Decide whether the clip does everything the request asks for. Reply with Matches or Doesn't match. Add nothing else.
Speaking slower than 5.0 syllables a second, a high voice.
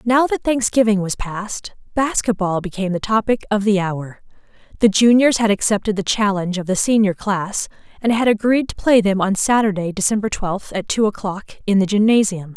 Doesn't match